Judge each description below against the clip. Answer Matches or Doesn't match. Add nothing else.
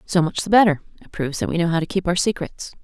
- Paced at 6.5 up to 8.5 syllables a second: Matches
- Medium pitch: Matches